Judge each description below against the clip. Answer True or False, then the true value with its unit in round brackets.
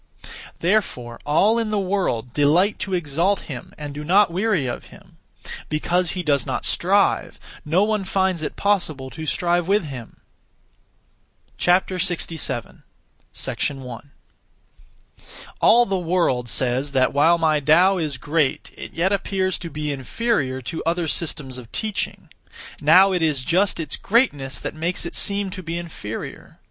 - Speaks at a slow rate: False (145 wpm)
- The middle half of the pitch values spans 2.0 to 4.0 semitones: False (4.9 semitones)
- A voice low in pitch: False (165 Hz)